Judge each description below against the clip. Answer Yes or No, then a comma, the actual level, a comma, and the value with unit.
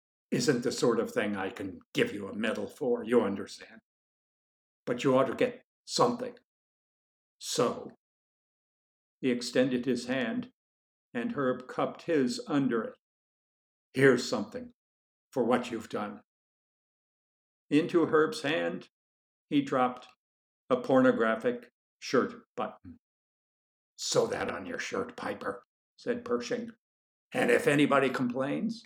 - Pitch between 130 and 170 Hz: Yes, medium, 140 Hz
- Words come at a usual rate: No, slow, 120 wpm